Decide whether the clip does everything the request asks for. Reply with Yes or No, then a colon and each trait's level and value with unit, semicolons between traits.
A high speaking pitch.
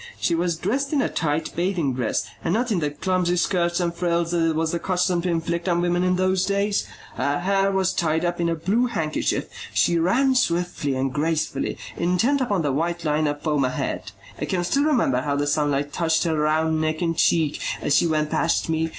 No: medium, 170 Hz